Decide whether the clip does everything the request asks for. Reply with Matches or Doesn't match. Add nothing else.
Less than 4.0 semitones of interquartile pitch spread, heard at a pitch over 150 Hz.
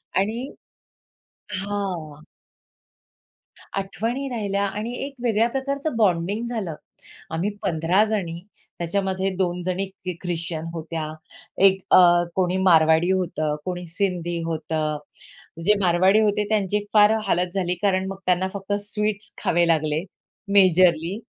Matches